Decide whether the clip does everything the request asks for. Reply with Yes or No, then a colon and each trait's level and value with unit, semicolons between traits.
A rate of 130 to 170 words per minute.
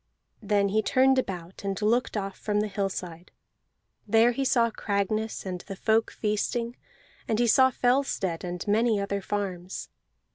Yes: average, 150 wpm